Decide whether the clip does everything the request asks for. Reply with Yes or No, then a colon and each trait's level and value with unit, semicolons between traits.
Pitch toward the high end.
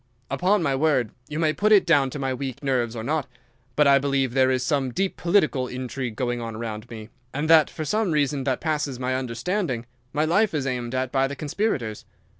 No: low, 135 Hz